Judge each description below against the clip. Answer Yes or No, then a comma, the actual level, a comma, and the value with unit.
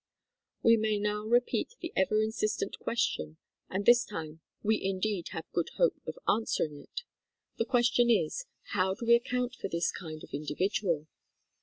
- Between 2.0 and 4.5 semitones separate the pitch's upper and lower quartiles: No, wide, 5.4 semitones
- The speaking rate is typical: Yes, average, 160 wpm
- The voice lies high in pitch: Yes, high, 210 Hz